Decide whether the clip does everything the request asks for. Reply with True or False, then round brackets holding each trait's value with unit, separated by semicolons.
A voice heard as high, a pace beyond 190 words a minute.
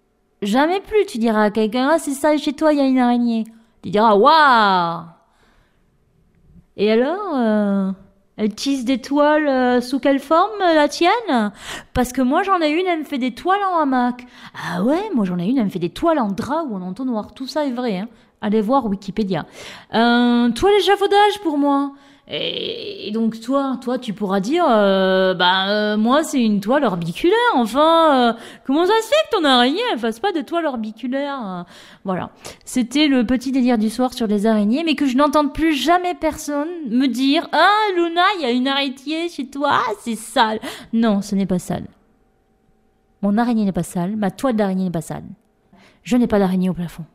True (250 Hz; 200 wpm)